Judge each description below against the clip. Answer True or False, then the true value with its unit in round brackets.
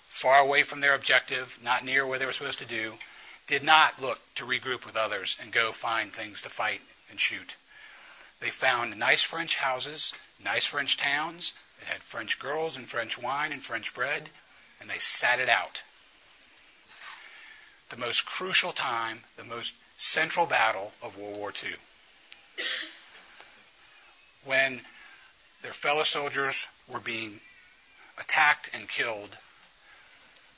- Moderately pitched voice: False (130 Hz)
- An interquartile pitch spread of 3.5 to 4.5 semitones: False (2.7 semitones)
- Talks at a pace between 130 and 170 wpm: True (140 wpm)